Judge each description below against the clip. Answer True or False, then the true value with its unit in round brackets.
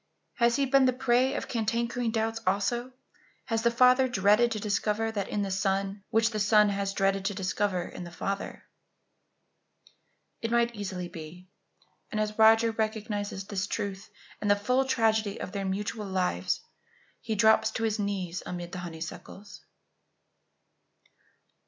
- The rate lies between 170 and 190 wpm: False (150 wpm)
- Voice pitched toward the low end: False (210 Hz)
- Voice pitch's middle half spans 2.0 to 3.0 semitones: True (2.6 semitones)